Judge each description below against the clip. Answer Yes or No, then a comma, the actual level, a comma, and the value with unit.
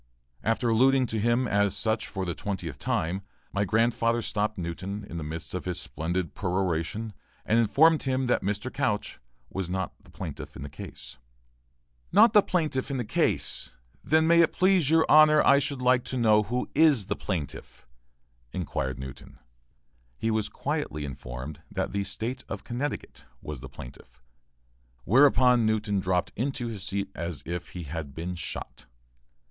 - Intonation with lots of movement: Yes, wide, 6.5 semitones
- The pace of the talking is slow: No, average, 160 wpm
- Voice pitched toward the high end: No, low, 105 Hz